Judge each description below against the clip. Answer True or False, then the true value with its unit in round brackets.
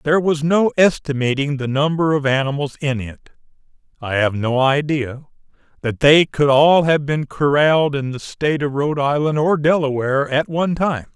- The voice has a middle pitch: True (145 Hz)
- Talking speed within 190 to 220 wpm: False (170 wpm)